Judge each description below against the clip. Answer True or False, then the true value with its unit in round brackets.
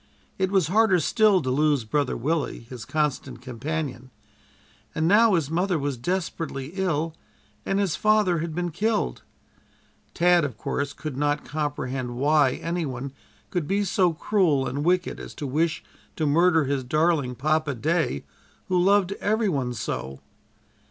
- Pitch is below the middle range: False (155 Hz)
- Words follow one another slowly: False (150 wpm)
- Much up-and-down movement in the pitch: False (4.5 semitones)